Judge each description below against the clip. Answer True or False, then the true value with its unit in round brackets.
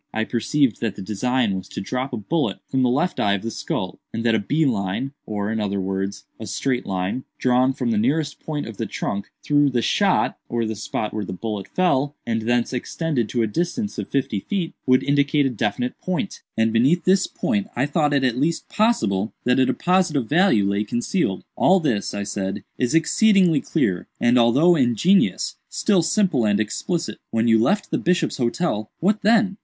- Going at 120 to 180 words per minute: False (200 wpm)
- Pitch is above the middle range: False (125 Hz)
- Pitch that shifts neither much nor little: False (7.1 semitones)